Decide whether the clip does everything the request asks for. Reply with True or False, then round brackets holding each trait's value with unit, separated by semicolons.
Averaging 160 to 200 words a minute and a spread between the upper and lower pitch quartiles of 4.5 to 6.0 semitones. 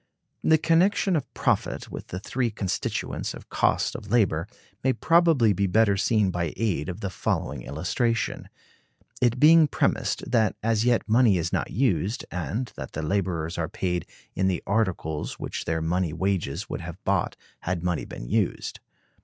True (165 wpm; 5.5 semitones)